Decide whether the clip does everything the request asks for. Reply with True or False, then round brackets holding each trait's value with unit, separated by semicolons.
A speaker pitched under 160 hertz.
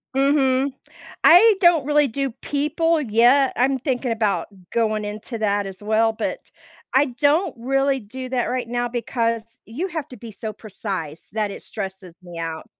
False (240 Hz)